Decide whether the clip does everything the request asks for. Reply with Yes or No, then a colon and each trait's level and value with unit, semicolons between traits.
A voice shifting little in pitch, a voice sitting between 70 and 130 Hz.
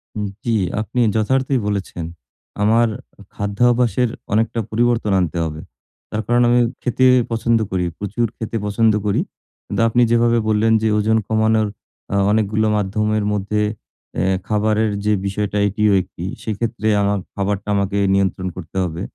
Yes: narrow, 2.2 semitones; low, 110 Hz